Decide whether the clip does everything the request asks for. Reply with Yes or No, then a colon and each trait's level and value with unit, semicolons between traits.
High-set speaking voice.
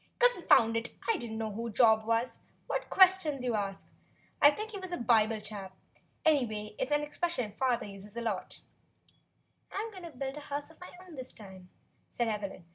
Yes: high, 240 Hz